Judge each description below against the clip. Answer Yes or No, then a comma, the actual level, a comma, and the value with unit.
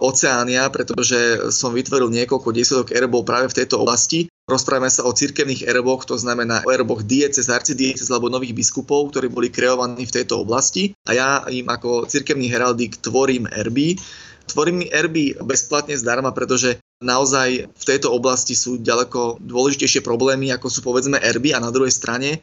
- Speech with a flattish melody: Yes, narrow, 1.8 semitones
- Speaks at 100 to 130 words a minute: No, average, 160 wpm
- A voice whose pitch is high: No, low, 130 Hz